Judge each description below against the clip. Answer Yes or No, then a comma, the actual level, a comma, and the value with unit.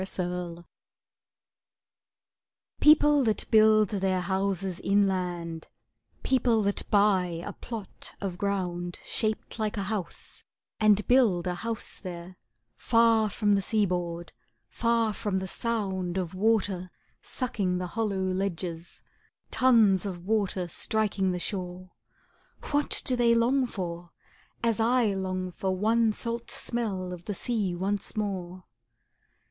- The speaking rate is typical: No, slow, 125 wpm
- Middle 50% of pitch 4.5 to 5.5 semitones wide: No, average, 3.5 semitones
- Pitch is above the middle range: Yes, high, 195 Hz